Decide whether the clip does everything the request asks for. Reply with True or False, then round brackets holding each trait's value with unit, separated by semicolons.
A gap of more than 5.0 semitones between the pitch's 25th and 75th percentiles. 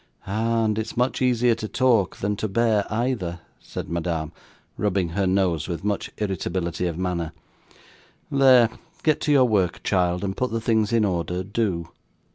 False (4.5 semitones)